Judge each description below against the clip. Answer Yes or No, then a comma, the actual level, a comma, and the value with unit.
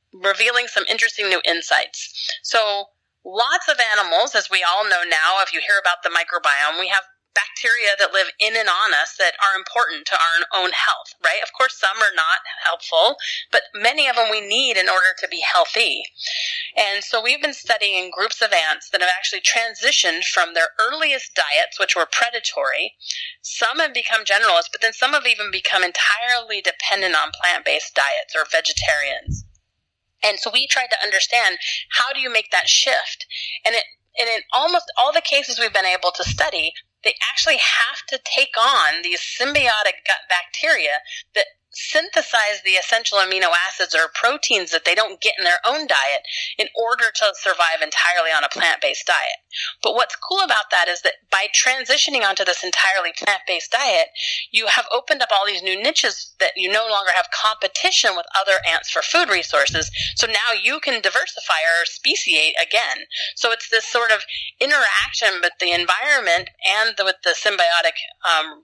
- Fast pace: No, average, 180 wpm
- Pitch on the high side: Yes, high, 230 Hz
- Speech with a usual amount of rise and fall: No, wide, 8.4 semitones